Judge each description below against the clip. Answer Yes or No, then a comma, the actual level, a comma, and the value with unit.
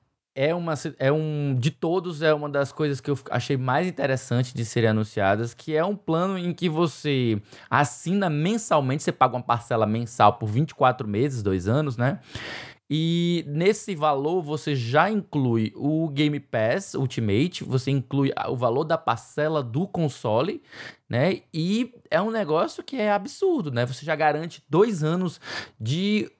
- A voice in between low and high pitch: Yes, medium, 150 Hz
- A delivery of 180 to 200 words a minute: No, average, 160 wpm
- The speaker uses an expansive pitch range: No, average, 5.0 semitones